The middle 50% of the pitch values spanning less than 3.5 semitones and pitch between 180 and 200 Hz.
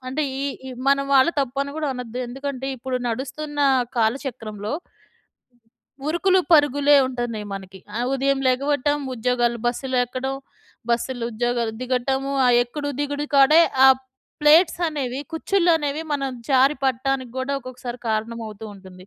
No: average, 3.0 semitones; very high, 260 Hz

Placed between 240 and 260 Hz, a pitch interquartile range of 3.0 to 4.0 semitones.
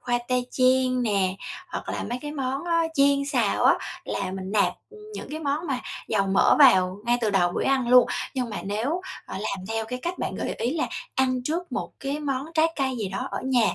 No: very high, 255 Hz; average, 4.6 semitones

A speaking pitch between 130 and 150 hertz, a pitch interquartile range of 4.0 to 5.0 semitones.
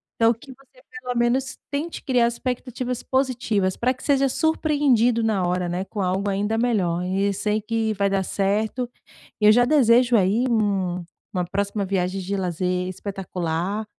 No: high, 220 Hz; average, 4.5 semitones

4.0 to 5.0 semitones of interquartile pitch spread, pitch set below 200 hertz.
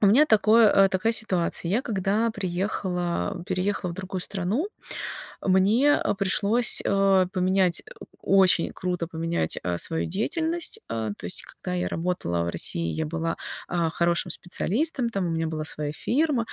Yes: average, 4.3 semitones; medium, 185 Hz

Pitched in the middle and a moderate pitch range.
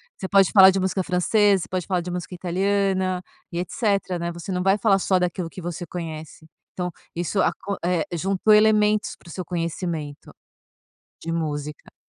No: medium, 180 Hz; narrow, 2.2 semitones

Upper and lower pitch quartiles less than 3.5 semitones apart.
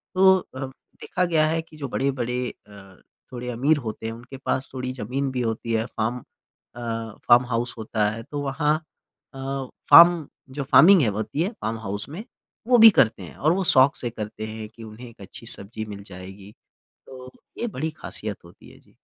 No: average, 4.6 semitones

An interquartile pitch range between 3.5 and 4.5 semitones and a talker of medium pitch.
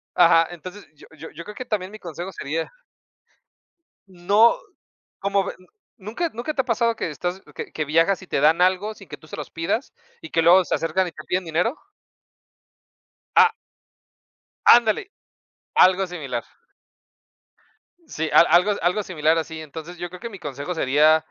Yes: average, 3.8 semitones; medium, 180 Hz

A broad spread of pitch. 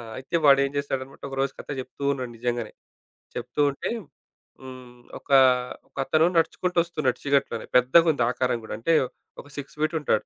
No: average, 2.7 semitones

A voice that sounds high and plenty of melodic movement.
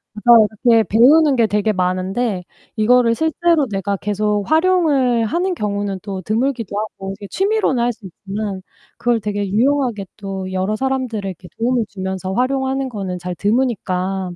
No: high, 215 Hz; average, 4.6 semitones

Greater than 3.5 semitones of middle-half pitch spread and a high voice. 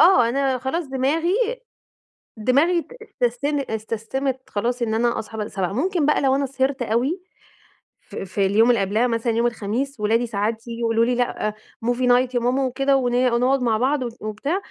No: average, 3.2 semitones; high, 245 Hz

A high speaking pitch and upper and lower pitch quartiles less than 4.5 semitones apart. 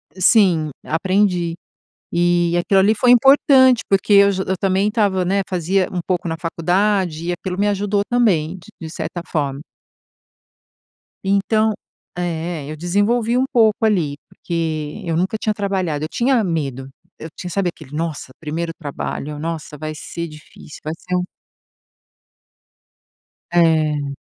No: medium, 180 Hz; average, 3.9 semitones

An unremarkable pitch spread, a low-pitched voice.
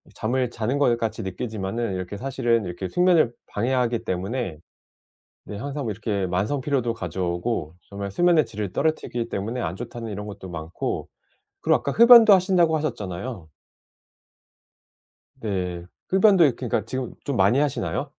No: wide, 5.7 semitones; low, 115 Hz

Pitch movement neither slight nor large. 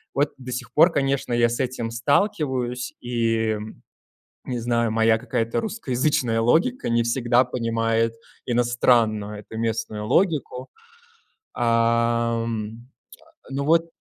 No: narrow, 2.3 semitones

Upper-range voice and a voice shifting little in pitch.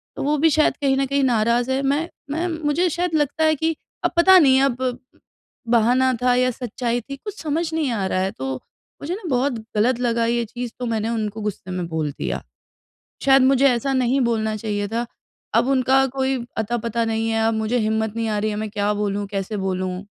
No: high, 240 Hz; average, 4.1 semitones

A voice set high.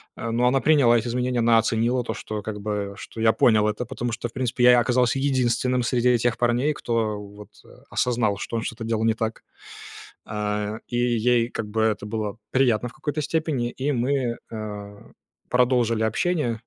No: low, 115 Hz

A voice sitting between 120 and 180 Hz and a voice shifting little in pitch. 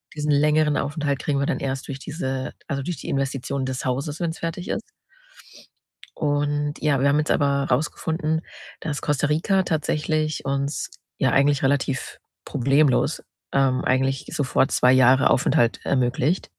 Yes: medium, 140 Hz; narrow, 2.2 semitones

